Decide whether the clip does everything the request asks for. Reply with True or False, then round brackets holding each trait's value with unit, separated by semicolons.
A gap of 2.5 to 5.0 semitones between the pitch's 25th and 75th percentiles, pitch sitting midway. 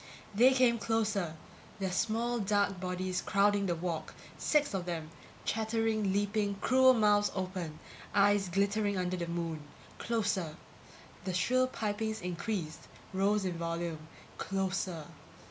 False (3.2 semitones; 200 Hz)